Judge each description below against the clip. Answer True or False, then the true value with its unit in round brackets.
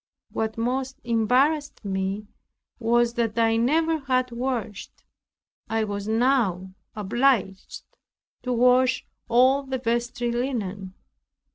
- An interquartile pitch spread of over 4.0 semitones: False (3.0 semitones)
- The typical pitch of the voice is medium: False (235 Hz)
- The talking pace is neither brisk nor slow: False (105 wpm)